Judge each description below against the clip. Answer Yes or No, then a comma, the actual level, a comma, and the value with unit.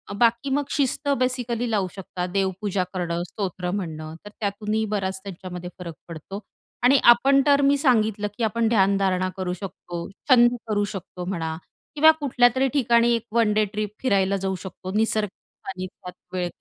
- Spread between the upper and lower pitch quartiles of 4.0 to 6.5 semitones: Yes, average, 4.3 semitones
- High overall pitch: Yes, high, 205 Hz